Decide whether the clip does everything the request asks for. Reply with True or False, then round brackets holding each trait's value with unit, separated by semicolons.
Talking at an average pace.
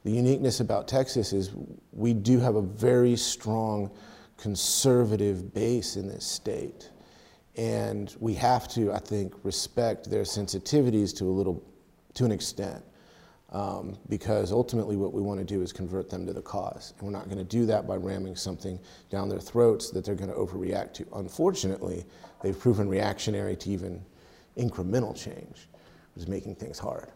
True (165 wpm)